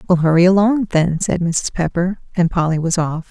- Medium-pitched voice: Yes, medium, 175 Hz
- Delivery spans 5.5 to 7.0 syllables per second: No, 5.1 syllables/s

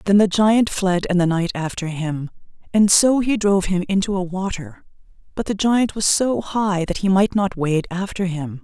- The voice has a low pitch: No, high, 190 Hz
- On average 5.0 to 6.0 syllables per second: No, 4.7 syllables/s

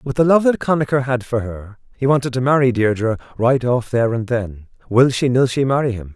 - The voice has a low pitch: Yes, low, 125 Hz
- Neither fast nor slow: No, fast, 235 wpm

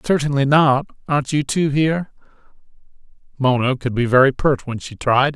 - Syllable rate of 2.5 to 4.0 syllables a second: No, 5.2 syllables/s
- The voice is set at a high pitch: No, medium, 140 Hz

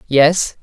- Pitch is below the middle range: No, medium, 155 Hz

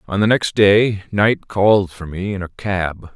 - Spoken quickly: Yes, fast, 210 wpm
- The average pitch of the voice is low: Yes, very low, 95 Hz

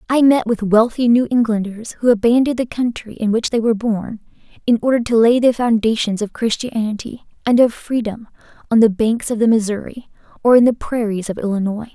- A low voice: No, high, 225 Hz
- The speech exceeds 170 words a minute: Yes, average, 190 wpm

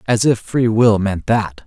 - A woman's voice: No, male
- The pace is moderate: No, fast, 215 wpm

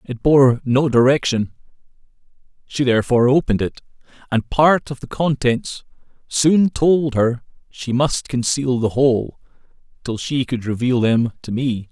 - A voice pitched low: Yes, low, 130 Hz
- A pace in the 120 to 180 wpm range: Yes, average, 140 wpm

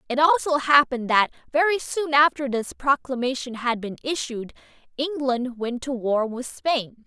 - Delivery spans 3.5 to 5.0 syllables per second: Yes, 4.5 syllables/s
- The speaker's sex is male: No, female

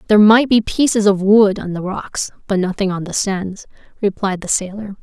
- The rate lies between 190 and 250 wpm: Yes, fast, 205 wpm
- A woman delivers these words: Yes, female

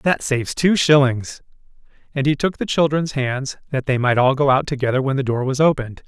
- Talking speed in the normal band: No, fast, 215 wpm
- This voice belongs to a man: Yes, male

